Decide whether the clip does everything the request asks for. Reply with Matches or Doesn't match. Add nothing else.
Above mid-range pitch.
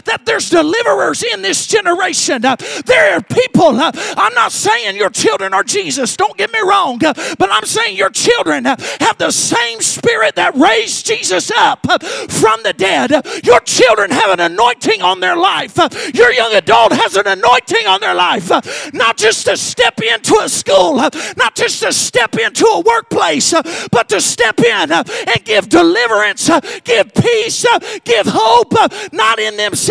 Matches